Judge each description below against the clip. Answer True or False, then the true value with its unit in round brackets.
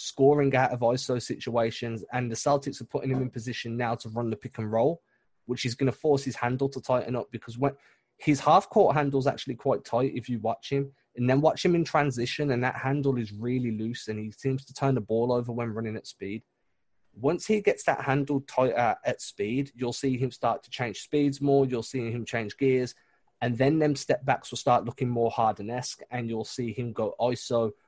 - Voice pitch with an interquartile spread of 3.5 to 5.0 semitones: False (2.7 semitones)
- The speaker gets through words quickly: True (230 wpm)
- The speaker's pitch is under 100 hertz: False (125 Hz)